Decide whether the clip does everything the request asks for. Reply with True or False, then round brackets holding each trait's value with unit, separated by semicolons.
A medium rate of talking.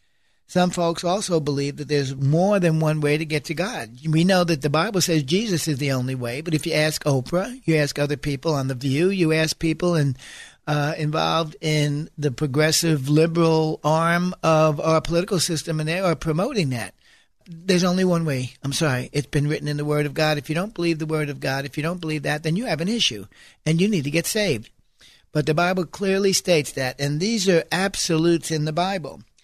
False (220 wpm)